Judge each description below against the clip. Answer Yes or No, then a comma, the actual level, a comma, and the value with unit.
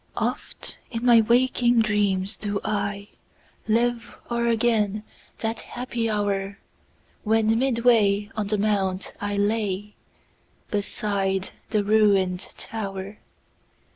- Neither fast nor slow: No, slow, 90 wpm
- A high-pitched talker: Yes, high, 210 Hz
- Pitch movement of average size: No, narrow, 2.2 semitones